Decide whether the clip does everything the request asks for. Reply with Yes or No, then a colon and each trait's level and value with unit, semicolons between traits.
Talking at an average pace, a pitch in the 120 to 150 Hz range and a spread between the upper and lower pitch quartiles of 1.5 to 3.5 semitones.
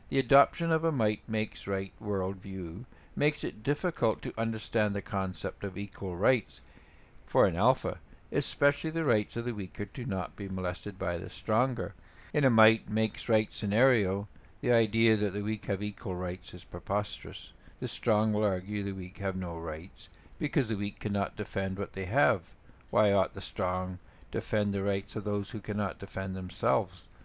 No: average, 175 wpm; low, 105 Hz; average, 2.9 semitones